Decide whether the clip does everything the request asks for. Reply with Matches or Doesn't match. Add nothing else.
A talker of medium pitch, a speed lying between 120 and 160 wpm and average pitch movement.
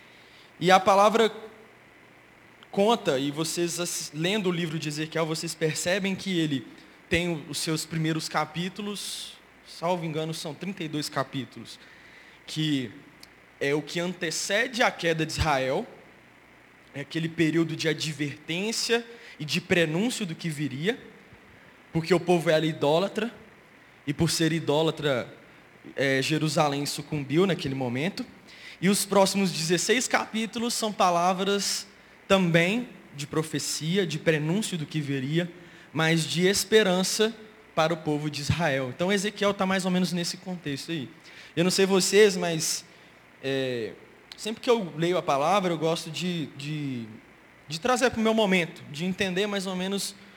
Matches